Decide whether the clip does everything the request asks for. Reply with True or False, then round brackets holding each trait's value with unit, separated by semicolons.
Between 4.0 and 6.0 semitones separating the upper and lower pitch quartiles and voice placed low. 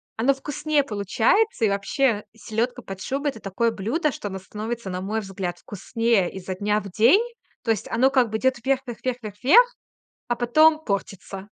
False (4.8 semitones; 225 Hz)